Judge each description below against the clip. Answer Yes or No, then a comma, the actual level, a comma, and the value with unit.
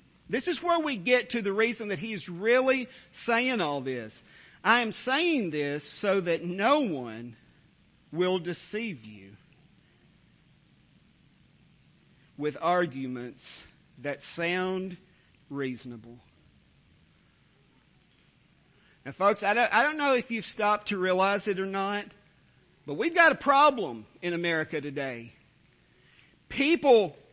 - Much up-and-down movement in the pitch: Yes, wide, 7.4 semitones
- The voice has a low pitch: No, medium, 185 Hz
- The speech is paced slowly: Yes, slow, 120 wpm